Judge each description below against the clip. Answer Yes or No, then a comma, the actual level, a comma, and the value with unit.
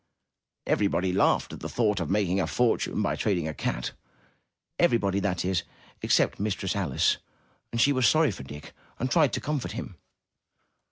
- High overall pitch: No, low, 100 Hz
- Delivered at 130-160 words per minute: No, average, 170 wpm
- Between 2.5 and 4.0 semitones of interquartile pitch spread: No, average, 4.5 semitones